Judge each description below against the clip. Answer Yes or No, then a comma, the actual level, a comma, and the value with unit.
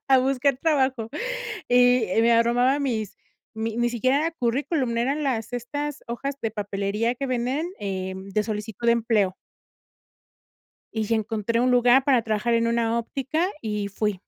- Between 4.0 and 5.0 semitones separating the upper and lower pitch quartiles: No, average, 3.1 semitones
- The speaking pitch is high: Yes, high, 235 Hz